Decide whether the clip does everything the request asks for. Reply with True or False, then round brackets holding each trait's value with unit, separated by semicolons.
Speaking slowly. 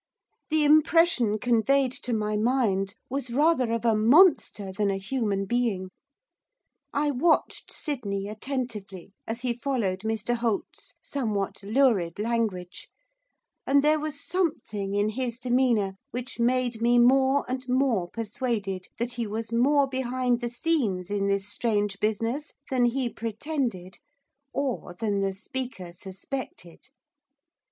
True (130 wpm)